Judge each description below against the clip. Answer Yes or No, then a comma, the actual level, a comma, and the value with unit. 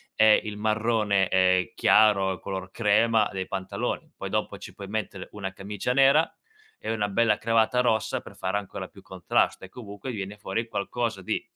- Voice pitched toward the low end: Yes, low, 105 Hz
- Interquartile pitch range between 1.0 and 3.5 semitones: Yes, narrow, 2.6 semitones